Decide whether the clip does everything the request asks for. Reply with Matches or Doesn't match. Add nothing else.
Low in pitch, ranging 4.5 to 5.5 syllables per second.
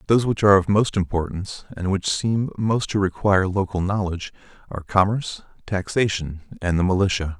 Doesn't match